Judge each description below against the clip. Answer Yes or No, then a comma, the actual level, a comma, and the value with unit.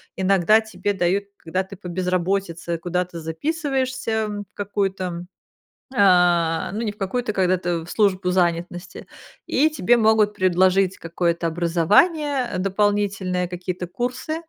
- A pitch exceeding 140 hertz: Yes, high, 190 Hz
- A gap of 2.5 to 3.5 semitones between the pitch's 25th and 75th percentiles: Yes, average, 3.1 semitones